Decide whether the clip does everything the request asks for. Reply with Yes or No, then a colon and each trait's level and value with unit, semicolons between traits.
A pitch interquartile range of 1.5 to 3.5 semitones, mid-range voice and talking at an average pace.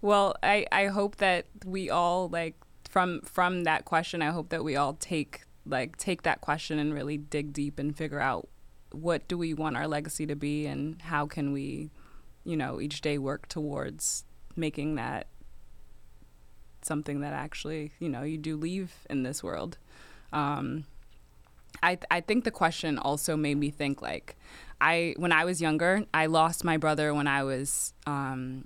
Yes: average, 2.7 semitones; medium, 150 Hz; average, 175 wpm